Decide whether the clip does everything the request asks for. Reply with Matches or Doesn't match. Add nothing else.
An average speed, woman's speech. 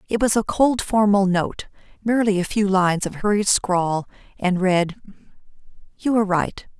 Matches